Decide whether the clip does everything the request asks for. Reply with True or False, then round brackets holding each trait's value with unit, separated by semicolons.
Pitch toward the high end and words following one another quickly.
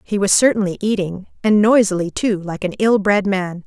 False (200 Hz; 195 wpm)